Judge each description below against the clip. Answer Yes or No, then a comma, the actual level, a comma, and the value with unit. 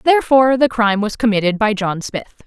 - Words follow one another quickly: No, average, 195 wpm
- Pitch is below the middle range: No, high, 225 Hz